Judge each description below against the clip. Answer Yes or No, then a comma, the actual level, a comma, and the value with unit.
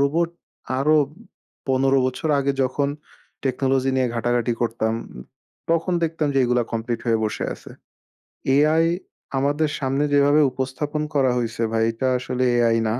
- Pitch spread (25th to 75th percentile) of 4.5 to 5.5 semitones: No, average, 3.3 semitones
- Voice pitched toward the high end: No, low, 135 Hz